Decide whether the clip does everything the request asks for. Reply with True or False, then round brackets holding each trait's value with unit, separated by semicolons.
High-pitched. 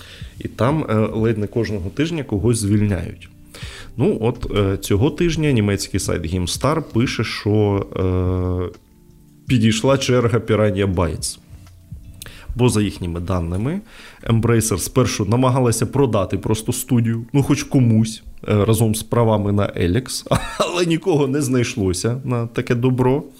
False (110 Hz)